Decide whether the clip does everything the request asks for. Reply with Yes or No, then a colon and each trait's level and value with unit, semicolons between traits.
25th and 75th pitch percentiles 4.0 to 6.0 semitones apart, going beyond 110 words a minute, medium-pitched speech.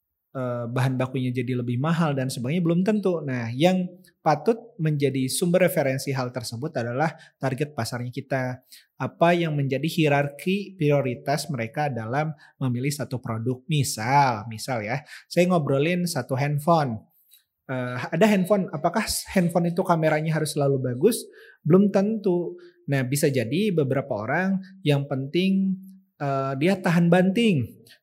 Yes: average, 5.3 semitones; average, 130 wpm; medium, 145 Hz